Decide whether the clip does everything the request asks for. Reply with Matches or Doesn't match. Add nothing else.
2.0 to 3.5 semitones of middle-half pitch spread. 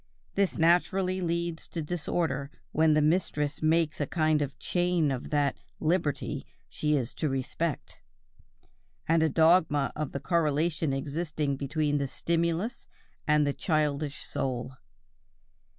Matches